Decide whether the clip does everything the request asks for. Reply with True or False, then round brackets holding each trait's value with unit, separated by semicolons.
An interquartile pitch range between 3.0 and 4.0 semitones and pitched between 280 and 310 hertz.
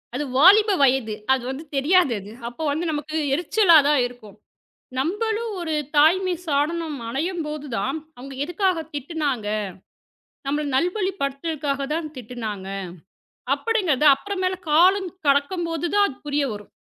False (4.5 semitones; 300 Hz)